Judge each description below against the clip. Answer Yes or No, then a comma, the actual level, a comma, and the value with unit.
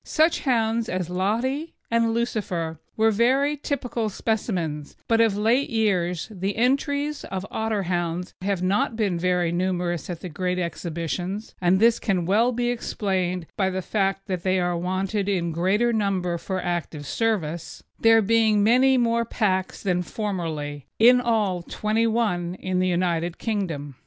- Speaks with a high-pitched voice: Yes, high, 195 Hz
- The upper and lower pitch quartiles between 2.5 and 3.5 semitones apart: No, average, 4.3 semitones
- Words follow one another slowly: No, average, 150 wpm